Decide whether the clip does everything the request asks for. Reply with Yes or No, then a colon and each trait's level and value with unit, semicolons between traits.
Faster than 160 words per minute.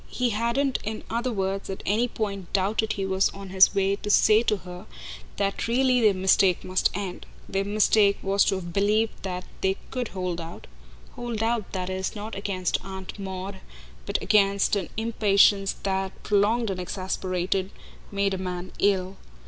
Yes: average, 170 wpm